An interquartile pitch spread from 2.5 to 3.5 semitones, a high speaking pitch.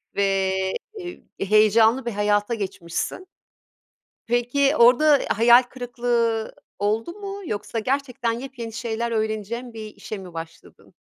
Yes: average, 2.8 semitones; high, 230 Hz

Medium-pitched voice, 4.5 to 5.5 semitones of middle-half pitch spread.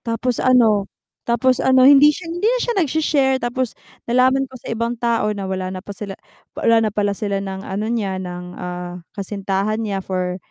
No: high, 220 Hz; average, 5.0 semitones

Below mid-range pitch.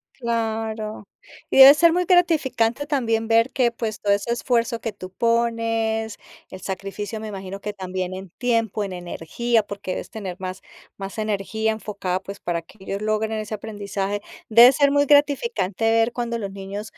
No: high, 220 Hz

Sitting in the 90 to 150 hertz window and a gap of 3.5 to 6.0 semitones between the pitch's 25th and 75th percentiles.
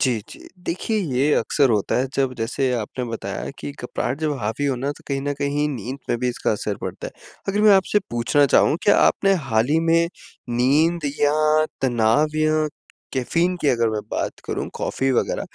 Yes: medium, 140 Hz; average, 4.4 semitones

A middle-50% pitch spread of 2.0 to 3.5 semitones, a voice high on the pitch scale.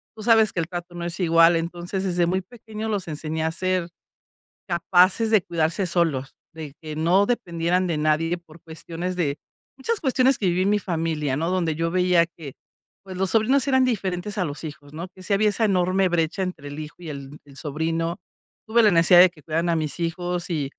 No: average, 2.8 semitones; medium, 175 Hz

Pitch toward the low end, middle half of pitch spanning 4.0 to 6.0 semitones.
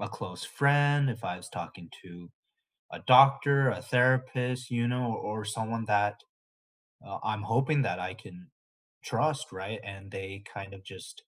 Yes: low, 115 Hz; average, 5.0 semitones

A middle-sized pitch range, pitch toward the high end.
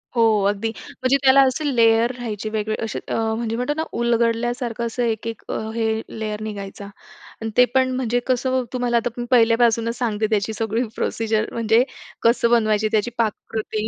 No: narrow, 1.8 semitones; high, 230 Hz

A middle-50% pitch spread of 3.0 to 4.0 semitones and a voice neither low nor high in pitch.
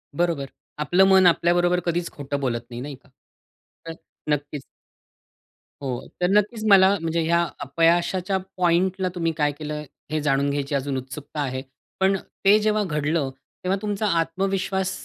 No: average, 4.8 semitones; medium, 165 Hz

